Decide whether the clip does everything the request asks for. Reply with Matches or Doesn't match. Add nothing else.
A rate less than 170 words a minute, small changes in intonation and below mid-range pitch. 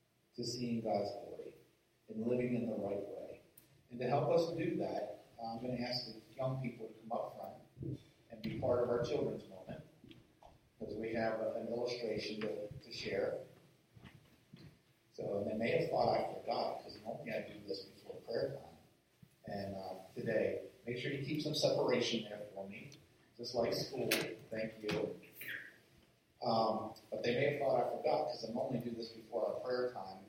Doesn't match